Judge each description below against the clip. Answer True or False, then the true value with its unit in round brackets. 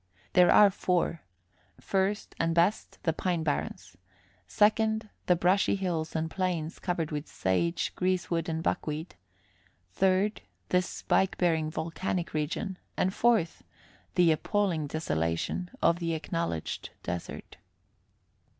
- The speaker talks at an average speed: False (115 wpm)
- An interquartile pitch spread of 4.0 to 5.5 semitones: False (2.9 semitones)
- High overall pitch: False (170 Hz)